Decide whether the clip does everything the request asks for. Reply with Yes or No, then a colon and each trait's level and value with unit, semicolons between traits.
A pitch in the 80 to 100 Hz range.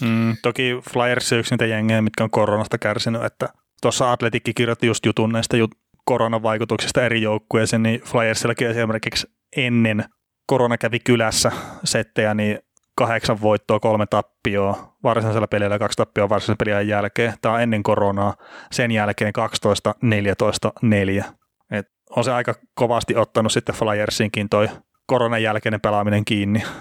No: low, 110 Hz